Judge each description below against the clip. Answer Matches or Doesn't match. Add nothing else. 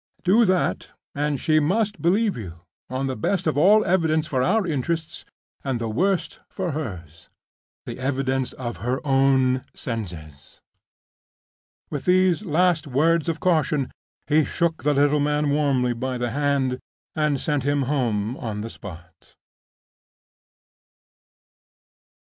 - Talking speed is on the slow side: Matches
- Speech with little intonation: Doesn't match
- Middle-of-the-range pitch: Matches